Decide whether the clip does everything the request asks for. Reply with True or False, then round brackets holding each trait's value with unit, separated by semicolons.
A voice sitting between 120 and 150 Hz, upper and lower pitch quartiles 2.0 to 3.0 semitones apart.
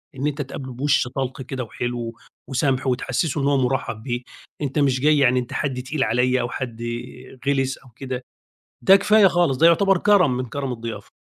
True (135 Hz; 2.5 semitones)